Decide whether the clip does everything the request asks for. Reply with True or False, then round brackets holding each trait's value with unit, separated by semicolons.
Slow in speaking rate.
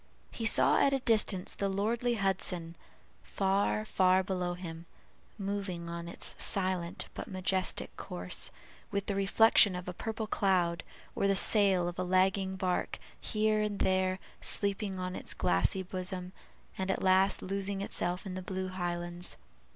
False (150 wpm)